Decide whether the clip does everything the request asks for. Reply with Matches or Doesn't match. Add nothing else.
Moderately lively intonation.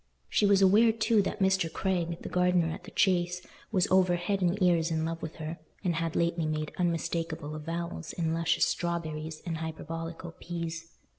Doesn't match